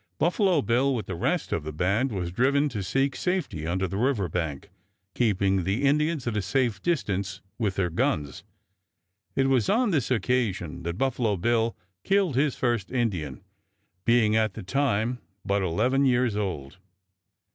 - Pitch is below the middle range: Yes, low, 115 Hz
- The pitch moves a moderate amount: No, wide, 6.1 semitones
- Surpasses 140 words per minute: Yes, average, 160 wpm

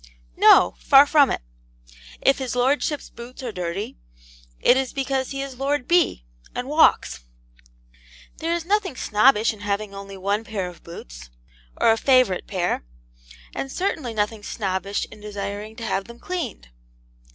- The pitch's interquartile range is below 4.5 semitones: No, wide, 5.4 semitones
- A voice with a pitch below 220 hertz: No, high, 225 Hz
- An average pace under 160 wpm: Yes, average, 150 wpm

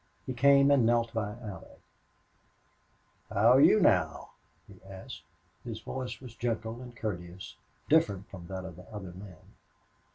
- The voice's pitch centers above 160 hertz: No, low, 110 Hz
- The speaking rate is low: No, average, 150 wpm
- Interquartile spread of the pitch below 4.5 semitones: No, average, 4.9 semitones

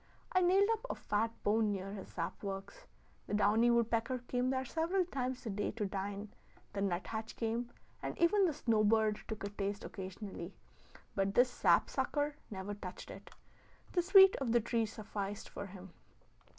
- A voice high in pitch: Yes, high, 220 Hz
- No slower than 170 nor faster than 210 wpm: Yes, average, 175 wpm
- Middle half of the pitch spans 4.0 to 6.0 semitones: Yes, average, 4.3 semitones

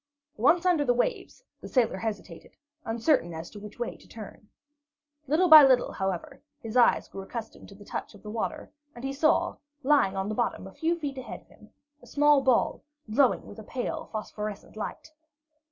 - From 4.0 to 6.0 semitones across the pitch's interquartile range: Yes, wide, 5.6 semitones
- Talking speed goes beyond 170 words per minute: Yes, average, 190 wpm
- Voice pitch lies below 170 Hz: No, high, 240 Hz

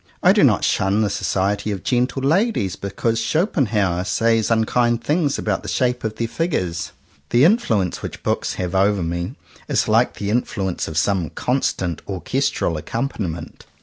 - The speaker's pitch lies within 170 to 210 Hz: No, low, 105 Hz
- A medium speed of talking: Yes, average, 160 wpm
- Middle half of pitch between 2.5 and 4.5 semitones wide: No, average, 5.0 semitones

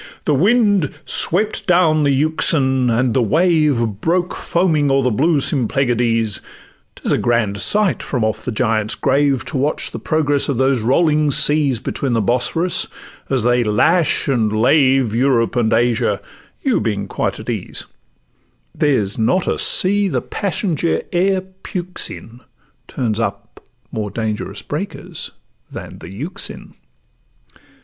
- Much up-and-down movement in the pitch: Yes, wide, 5.9 semitones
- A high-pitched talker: No, low, 135 Hz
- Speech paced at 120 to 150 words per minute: Yes, average, 140 wpm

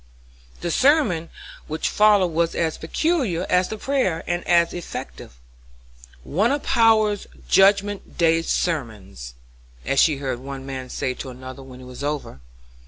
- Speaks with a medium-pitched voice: Yes, medium, 165 Hz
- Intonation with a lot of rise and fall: Yes, wide, 7.2 semitones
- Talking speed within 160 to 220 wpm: No, average, 145 wpm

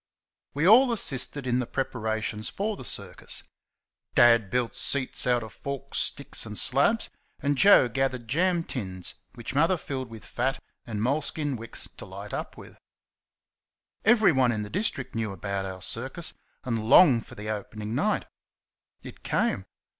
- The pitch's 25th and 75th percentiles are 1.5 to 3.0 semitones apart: No, average, 4.8 semitones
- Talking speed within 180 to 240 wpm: No, average, 155 wpm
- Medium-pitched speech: No, low, 125 Hz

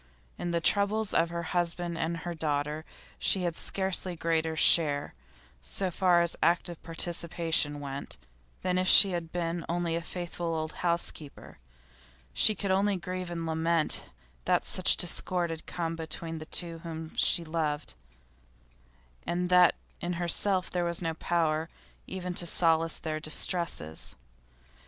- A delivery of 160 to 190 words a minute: No, average, 140 wpm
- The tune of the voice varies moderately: No, narrow, 1.6 semitones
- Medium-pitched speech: Yes, medium, 170 Hz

